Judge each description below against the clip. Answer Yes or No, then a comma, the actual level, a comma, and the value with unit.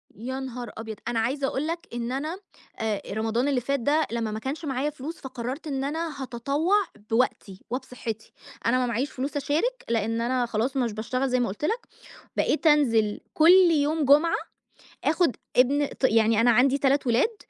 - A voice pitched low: No, very high, 260 Hz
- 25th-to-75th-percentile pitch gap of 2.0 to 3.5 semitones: No, average, 4.0 semitones